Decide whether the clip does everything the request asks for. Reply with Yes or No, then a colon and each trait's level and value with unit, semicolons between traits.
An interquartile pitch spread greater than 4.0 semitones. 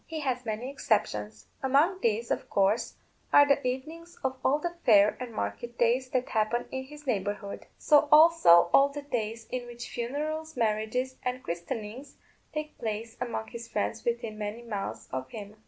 Yes: average, 4.5 semitones